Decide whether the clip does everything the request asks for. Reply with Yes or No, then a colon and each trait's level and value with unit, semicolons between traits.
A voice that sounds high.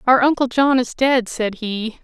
Yes: high, 245 Hz